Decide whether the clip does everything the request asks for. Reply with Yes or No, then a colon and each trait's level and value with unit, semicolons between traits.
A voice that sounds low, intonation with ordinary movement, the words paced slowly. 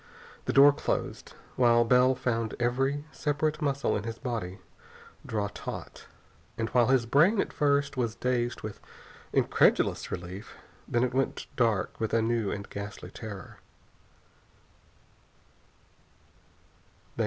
Yes: low, 120 Hz; average, 3.3 semitones; slow, 120 wpm